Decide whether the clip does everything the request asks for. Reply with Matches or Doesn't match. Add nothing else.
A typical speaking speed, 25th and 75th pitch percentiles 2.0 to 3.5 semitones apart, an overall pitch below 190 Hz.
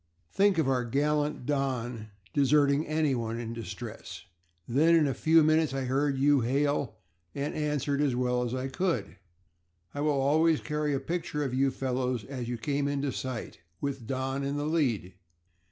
Matches